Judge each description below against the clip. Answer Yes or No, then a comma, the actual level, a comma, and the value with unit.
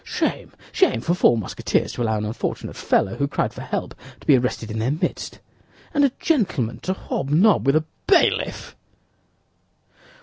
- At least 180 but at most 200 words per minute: No, average, 165 wpm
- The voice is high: No, medium, 140 Hz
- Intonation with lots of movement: Yes, wide, 8.3 semitones